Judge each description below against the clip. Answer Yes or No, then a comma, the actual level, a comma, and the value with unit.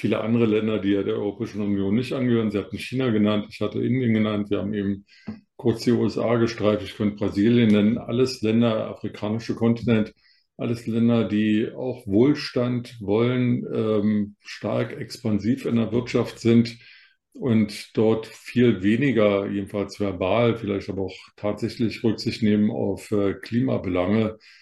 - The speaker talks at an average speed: Yes, average, 150 wpm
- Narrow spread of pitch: Yes, narrow, 2.2 semitones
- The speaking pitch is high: No, low, 110 Hz